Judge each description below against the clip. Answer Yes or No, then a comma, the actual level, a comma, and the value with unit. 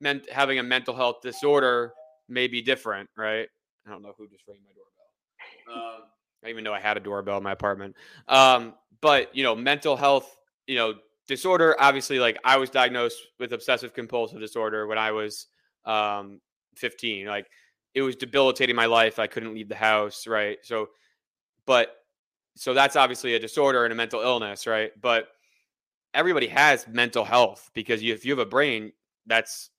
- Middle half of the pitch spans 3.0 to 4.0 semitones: Yes, average, 3.3 semitones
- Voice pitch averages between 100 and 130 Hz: Yes, low, 115 Hz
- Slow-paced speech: No, average, 180 wpm